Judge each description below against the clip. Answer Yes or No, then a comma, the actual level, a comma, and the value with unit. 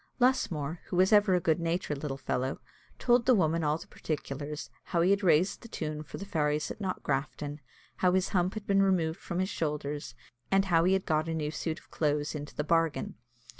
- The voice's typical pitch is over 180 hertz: No, medium, 165 Hz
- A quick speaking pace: Yes, fast, 210 wpm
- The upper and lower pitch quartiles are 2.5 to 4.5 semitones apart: Yes, average, 4.0 semitones